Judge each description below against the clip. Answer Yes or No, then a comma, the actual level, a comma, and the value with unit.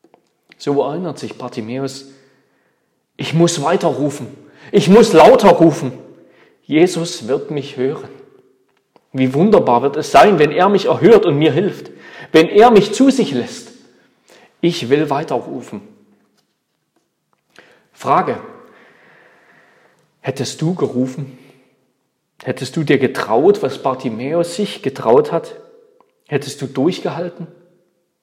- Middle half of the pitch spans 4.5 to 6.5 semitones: Yes, average, 5.1 semitones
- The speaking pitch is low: No, medium, 160 Hz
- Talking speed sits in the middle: No, slow, 110 wpm